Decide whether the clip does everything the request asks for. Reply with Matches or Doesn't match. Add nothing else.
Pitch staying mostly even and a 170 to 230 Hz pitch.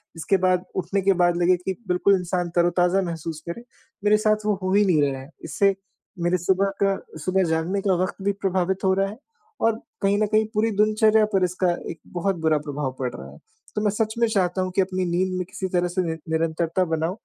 Matches